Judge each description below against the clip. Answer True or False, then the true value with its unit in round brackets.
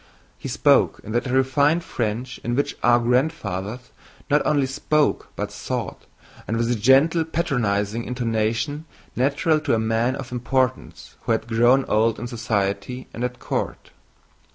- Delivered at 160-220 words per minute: False (150 wpm)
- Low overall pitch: True (125 Hz)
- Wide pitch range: False (3.2 semitones)